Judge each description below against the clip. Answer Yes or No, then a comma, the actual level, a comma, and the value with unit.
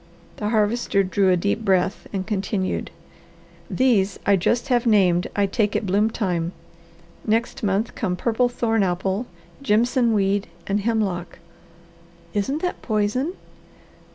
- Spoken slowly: Yes, slow, 130 wpm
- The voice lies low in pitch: No, high, 210 Hz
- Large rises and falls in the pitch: No, average, 3.2 semitones